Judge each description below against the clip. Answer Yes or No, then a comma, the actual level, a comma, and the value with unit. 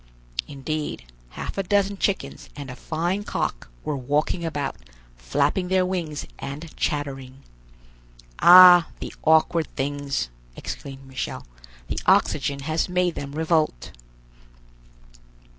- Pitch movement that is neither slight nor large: Yes, average, 4.2 semitones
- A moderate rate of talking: No, slow, 110 wpm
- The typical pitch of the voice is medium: Yes, medium, 155 Hz